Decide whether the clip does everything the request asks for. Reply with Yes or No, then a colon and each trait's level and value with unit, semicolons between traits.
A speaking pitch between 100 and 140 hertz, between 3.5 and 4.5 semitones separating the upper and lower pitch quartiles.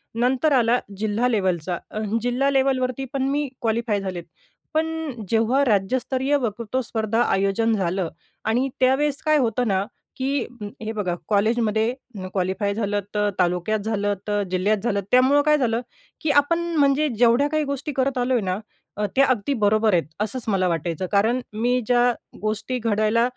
No: high, 230 Hz; average, 4.1 semitones